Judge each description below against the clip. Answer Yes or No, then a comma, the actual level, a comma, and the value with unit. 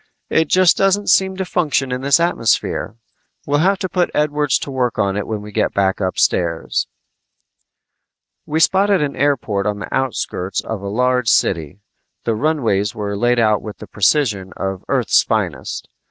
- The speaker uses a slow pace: No, average, 170 wpm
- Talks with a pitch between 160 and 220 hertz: No, low, 125 Hz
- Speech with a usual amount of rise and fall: No, wide, 6.9 semitones